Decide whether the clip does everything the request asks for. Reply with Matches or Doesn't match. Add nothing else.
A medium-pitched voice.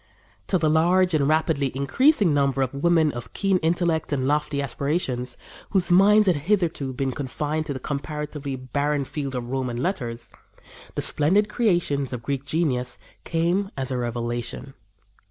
Matches